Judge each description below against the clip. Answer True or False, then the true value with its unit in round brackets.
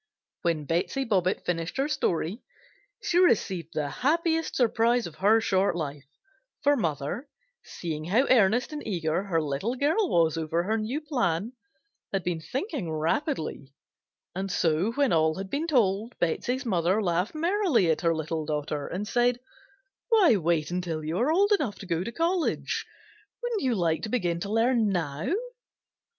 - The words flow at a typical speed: True (160 wpm)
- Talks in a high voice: True (195 Hz)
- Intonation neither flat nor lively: False (7.7 semitones)